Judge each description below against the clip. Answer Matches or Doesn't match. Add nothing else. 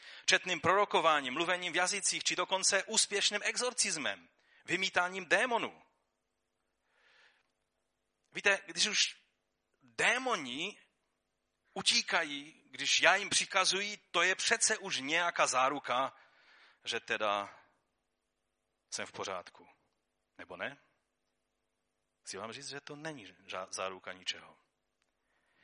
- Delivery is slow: Matches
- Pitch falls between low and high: Matches